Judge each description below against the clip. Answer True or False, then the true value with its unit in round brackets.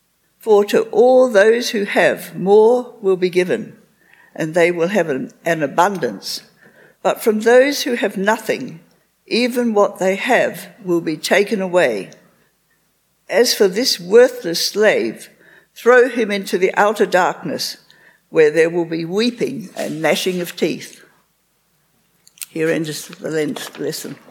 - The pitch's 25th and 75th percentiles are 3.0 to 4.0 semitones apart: False (5.2 semitones)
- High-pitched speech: True (205 Hz)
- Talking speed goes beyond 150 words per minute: False (135 wpm)